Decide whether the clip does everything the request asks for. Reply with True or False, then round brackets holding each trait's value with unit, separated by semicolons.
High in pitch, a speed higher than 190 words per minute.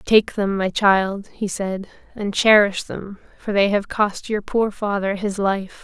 False (200 Hz; 185 wpm)